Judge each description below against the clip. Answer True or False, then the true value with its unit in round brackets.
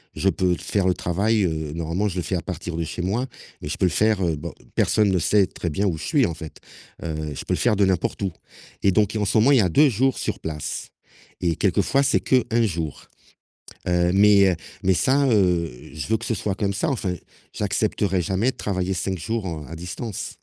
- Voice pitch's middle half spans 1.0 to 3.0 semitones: False (3.7 semitones)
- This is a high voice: False (95 Hz)